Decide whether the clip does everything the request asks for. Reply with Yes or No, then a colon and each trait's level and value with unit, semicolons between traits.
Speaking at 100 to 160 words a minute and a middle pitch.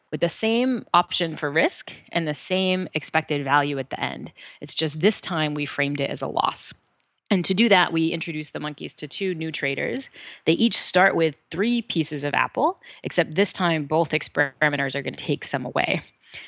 No: average, 195 wpm; medium, 160 Hz